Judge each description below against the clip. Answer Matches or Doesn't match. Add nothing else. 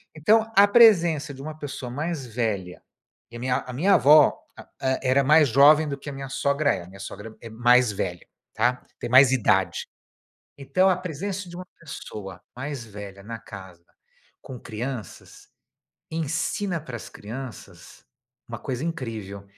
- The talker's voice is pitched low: Matches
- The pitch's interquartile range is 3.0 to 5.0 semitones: Doesn't match